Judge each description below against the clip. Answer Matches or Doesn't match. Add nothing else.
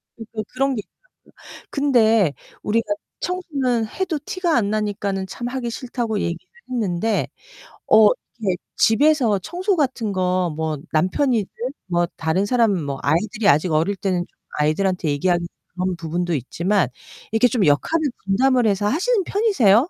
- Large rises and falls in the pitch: Matches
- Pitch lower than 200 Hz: Doesn't match